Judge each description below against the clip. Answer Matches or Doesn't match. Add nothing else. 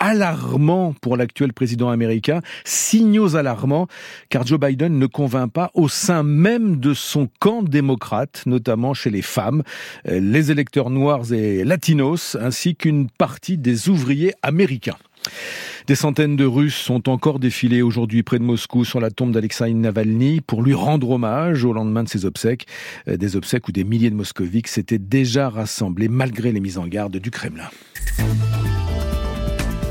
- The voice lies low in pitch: Matches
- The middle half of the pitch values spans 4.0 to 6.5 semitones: Matches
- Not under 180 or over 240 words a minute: Doesn't match